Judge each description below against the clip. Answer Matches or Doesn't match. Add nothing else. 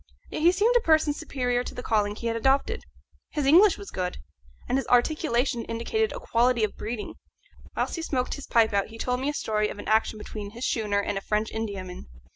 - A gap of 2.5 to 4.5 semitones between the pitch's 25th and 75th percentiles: Doesn't match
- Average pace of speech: Doesn't match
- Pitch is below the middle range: Doesn't match